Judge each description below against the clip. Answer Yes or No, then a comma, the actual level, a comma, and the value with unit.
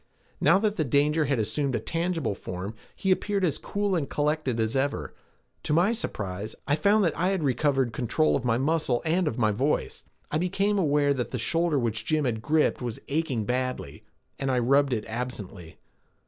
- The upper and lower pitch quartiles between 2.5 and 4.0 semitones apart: No, wide, 5.4 semitones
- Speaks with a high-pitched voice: No, medium, 140 Hz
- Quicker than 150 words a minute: Yes, average, 190 wpm